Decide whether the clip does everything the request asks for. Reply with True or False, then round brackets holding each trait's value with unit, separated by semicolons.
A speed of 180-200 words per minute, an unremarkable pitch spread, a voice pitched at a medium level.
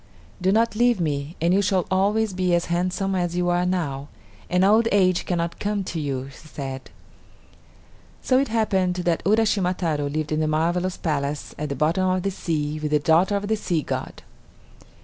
True (190 wpm; 3.9 semitones; 180 Hz)